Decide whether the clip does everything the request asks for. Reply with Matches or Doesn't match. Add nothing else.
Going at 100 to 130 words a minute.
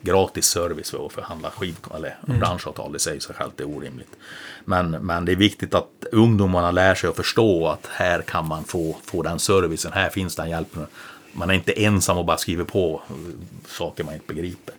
Doesn't match